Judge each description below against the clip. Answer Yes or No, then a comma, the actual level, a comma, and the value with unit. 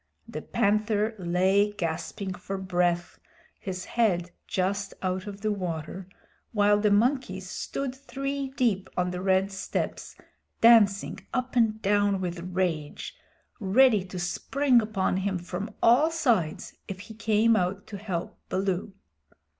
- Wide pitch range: No, average, 3.2 semitones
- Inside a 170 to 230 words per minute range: No, slow, 135 wpm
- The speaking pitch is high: Yes, high, 200 Hz